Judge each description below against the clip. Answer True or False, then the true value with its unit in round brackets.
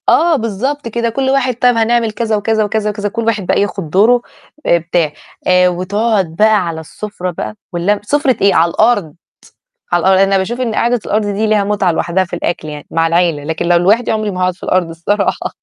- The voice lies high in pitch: True (205 Hz)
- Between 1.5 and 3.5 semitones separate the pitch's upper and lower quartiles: False (4.3 semitones)